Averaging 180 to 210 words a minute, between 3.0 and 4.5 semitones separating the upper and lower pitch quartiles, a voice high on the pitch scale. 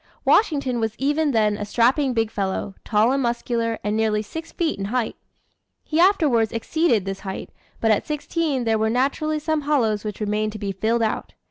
No: average, 190 wpm; average, 5.3 semitones; high, 230 Hz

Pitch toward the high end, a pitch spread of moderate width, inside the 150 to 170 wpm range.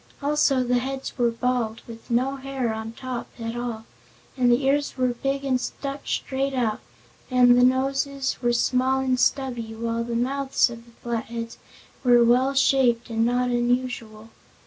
No: very high, 250 Hz; narrow, 2.2 semitones; average, 165 wpm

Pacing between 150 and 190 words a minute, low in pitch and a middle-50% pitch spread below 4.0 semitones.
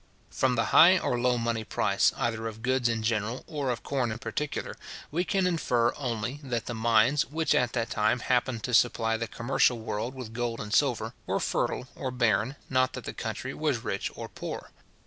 No: average, 200 wpm; low, 120 Hz; narrow, 2.6 semitones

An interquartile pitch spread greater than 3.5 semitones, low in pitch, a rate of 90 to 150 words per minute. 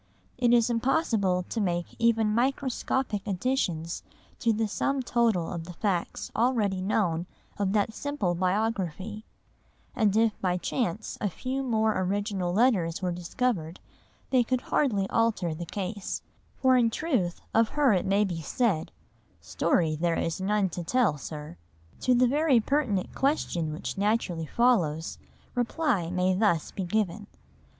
No: average, 5.1 semitones; high, 205 Hz; average, 145 wpm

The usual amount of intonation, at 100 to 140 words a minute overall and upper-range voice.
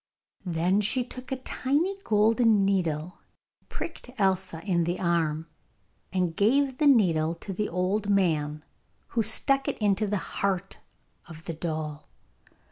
Yes: average, 5.0 semitones; slow, 135 wpm; high, 195 Hz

